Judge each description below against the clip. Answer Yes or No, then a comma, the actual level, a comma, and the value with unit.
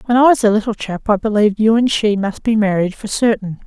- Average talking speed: No, fast, 260 wpm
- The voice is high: Yes, high, 215 Hz